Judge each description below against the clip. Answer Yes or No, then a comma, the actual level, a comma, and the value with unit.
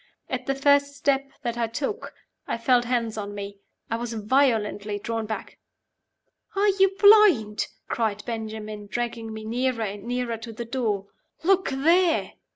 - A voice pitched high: Yes, high, 235 Hz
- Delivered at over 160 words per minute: No, average, 155 wpm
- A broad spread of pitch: No, average, 3.9 semitones